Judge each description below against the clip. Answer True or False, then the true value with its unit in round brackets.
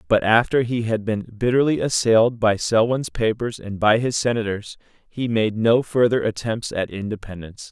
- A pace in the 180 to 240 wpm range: False (165 wpm)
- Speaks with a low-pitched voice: True (115 Hz)